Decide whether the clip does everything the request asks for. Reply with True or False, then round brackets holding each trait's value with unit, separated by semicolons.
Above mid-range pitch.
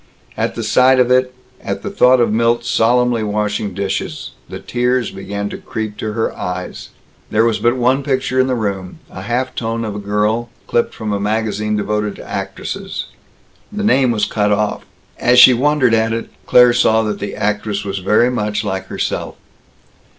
False (110 Hz)